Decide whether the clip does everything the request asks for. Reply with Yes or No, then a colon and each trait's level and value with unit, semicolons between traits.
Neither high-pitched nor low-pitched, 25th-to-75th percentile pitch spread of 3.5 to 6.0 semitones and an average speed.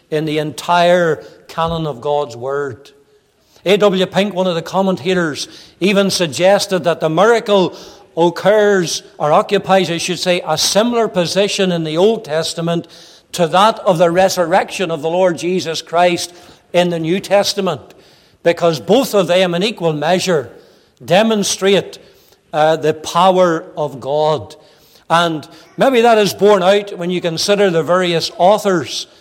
No: medium, 180 Hz; average, 3.0 semitones; average, 145 wpm